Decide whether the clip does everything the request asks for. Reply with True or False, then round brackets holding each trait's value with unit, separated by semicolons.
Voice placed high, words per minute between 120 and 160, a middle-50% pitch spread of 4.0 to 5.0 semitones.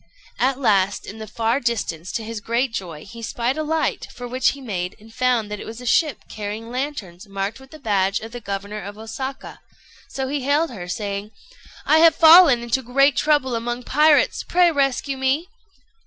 False (240 Hz; 195 wpm; 4.7 semitones)